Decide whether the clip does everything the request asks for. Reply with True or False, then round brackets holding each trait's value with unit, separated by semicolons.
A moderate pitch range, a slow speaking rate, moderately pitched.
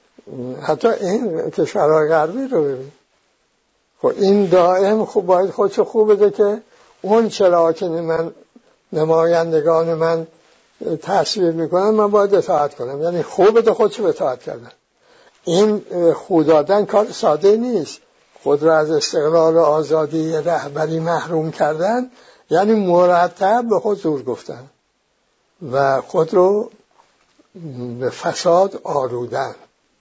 True (4.7 semitones; 125 wpm; 175 Hz)